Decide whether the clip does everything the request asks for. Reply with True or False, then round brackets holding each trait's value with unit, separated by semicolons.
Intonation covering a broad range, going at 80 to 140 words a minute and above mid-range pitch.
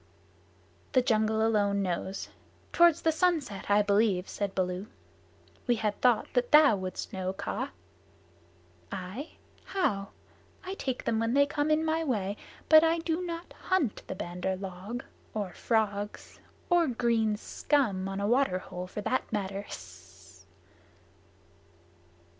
True (6.6 semitones; 135 wpm; 220 Hz)